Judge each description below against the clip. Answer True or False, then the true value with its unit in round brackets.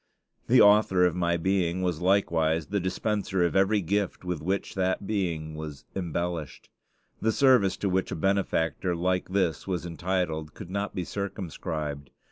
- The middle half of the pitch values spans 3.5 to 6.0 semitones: False (2.9 semitones)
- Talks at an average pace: True (155 wpm)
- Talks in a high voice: False (90 Hz)